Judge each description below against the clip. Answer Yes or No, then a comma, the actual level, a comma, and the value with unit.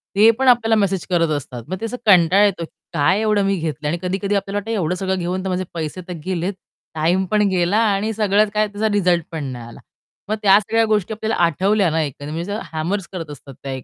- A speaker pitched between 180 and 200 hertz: Yes, high, 190 Hz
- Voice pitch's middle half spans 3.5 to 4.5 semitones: Yes, average, 3.9 semitones